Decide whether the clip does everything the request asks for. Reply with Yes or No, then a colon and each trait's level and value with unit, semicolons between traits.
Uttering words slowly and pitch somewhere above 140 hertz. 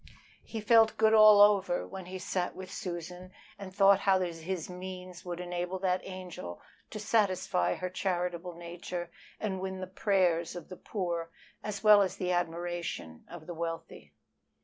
No: average, 160 wpm; medium, 185 Hz